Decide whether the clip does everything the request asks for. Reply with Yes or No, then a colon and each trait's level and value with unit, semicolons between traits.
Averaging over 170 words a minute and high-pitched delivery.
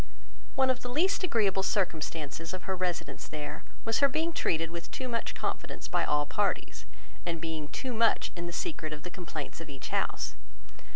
No: average, 185 wpm; medium, 175 Hz